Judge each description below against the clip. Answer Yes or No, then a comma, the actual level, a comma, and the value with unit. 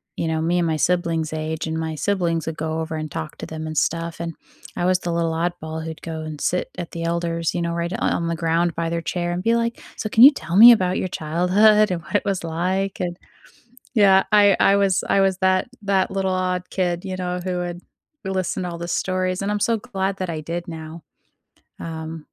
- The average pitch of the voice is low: No, medium, 175 Hz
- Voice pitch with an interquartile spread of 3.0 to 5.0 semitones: No, narrow, 2.5 semitones